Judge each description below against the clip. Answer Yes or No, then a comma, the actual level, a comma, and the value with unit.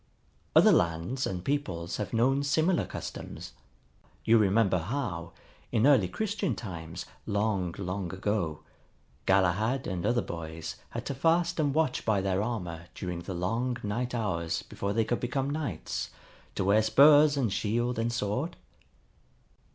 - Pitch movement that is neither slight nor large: No, wide, 6.0 semitones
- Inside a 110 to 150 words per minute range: Yes, average, 145 wpm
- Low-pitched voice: Yes, low, 110 Hz